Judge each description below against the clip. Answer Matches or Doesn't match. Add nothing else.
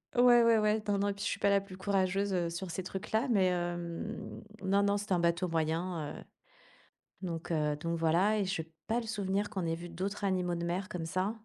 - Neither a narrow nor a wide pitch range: Matches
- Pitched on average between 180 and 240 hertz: Matches